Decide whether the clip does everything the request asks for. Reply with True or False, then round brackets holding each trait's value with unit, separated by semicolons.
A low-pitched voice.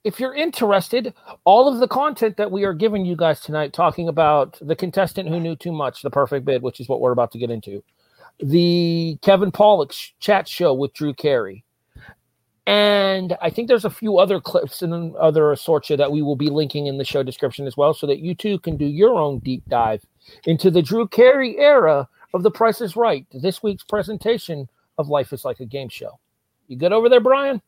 False (170 Hz)